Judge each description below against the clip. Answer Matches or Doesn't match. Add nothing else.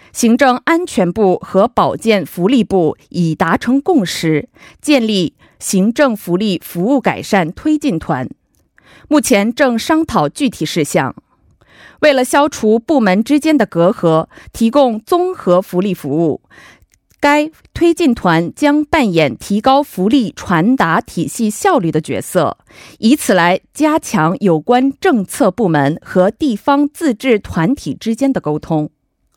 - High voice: Matches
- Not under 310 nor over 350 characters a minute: Doesn't match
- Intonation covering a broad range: Matches